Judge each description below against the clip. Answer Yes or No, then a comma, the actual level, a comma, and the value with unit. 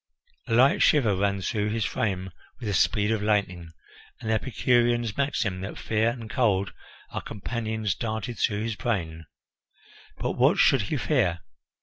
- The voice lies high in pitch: No, low, 110 Hz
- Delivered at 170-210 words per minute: No, average, 155 wpm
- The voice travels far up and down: No, average, 3.0 semitones